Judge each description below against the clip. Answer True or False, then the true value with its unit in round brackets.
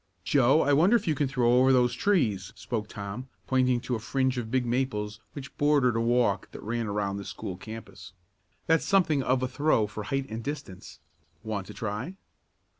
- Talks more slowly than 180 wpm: False (190 wpm)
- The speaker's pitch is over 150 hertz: False (125 Hz)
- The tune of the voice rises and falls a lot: False (4.1 semitones)